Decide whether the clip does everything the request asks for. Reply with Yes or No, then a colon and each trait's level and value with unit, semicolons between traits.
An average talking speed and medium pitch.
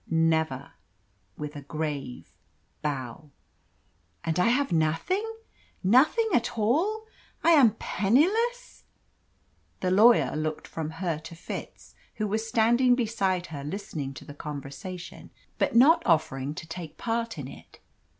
No: slow, 130 wpm; medium, 180 Hz